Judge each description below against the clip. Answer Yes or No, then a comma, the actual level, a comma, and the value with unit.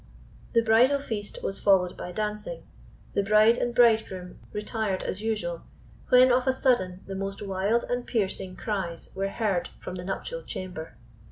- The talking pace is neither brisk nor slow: Yes, average, 160 wpm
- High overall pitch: Yes, high, 210 Hz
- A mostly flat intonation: No, average, 3.8 semitones